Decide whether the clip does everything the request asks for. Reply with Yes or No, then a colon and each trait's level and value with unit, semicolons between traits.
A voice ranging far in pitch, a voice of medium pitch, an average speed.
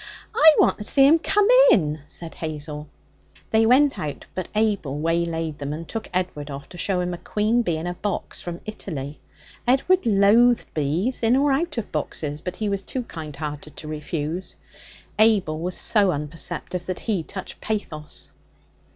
Yes: wide, 6.3 semitones; medium, 180 Hz; average, 175 wpm